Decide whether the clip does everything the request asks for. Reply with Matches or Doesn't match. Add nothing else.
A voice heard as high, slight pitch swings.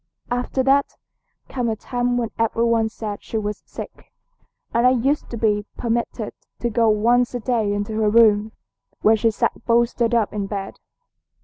Matches